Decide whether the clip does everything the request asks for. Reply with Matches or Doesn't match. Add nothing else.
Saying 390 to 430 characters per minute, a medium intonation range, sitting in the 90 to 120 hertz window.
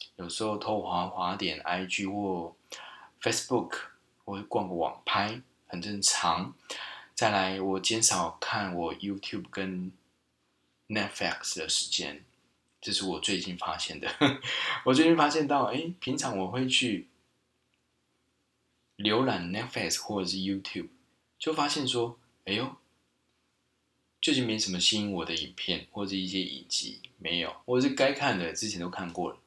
Doesn't match